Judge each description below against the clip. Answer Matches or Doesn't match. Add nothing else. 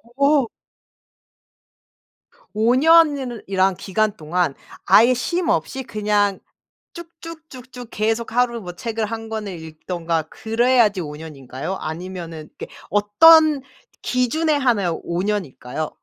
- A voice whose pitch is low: Doesn't match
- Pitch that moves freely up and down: Matches